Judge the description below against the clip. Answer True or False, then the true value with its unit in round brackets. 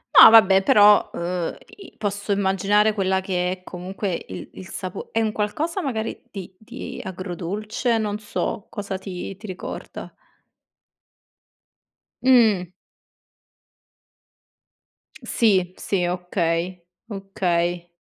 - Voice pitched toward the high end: True (195 Hz)